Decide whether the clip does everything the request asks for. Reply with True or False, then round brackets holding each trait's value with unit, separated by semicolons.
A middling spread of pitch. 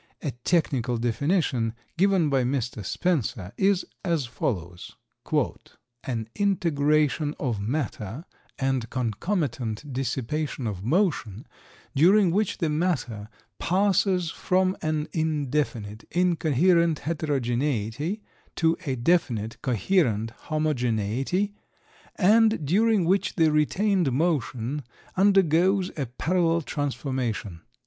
False (6.6 semitones)